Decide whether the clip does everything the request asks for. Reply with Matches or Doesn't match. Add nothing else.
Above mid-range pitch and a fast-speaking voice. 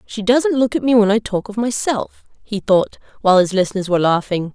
Matches